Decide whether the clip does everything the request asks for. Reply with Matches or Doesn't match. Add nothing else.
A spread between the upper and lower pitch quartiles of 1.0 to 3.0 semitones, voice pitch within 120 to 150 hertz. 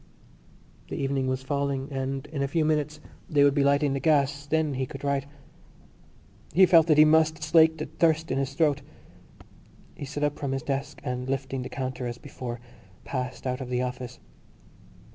Matches